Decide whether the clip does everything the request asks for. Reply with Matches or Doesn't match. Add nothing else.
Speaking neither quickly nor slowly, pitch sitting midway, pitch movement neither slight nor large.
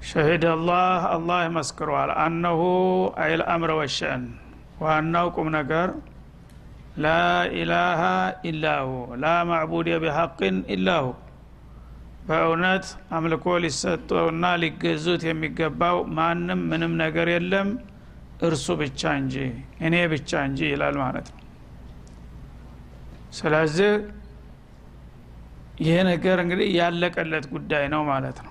Matches